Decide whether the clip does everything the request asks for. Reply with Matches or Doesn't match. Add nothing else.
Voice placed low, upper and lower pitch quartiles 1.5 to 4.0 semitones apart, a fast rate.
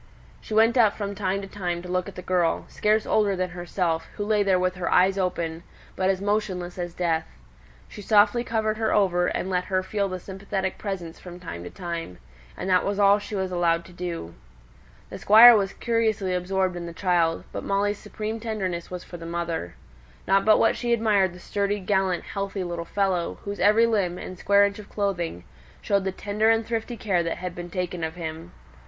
Doesn't match